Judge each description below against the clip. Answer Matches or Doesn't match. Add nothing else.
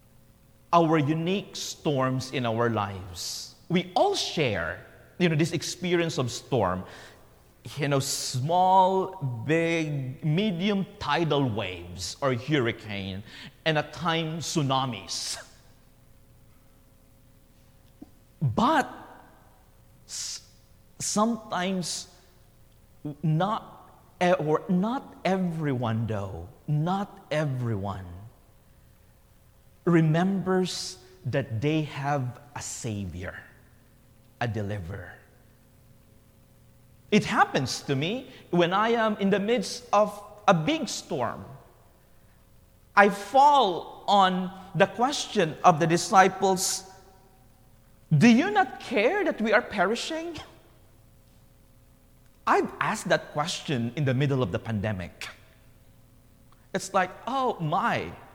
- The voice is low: Doesn't match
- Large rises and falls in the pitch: Matches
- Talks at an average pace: Doesn't match